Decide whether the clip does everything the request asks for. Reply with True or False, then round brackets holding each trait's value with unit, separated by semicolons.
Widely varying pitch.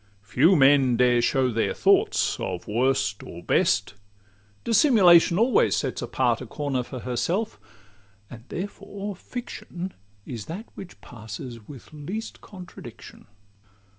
True (8.1 semitones)